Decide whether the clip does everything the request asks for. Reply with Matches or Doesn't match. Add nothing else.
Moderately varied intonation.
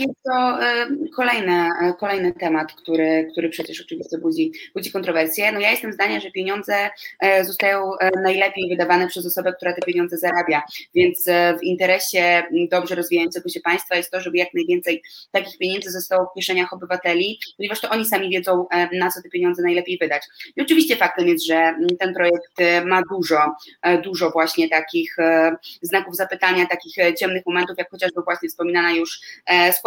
Doesn't match